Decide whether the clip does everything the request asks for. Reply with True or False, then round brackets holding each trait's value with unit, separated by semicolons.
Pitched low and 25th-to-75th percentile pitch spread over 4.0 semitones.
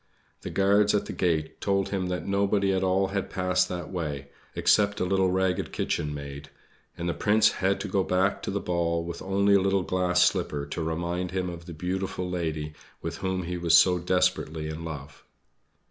False (90 Hz; 2.5 semitones)